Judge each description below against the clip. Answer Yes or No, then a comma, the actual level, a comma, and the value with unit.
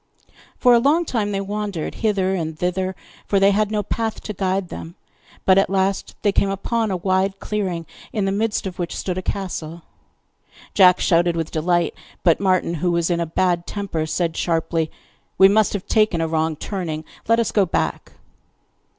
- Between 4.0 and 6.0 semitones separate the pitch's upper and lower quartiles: No, average, 3.0 semitones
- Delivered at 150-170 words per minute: No, average, 185 wpm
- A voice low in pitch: No, high, 190 Hz